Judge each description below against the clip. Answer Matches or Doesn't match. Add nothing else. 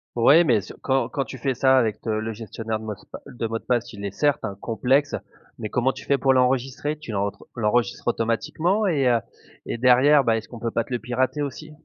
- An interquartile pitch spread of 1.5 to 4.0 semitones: Matches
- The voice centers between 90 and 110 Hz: Doesn't match